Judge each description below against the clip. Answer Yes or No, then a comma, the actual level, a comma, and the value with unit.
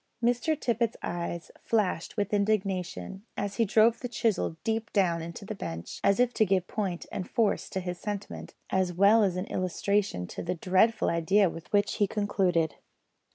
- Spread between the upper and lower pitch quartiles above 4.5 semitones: No, average, 3.3 semitones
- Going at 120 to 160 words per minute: No, average, 175 wpm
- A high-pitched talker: Yes, high, 200 Hz